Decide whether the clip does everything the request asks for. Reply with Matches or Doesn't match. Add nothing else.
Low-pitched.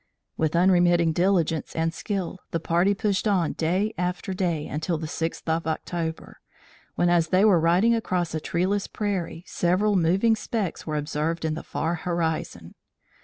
Doesn't match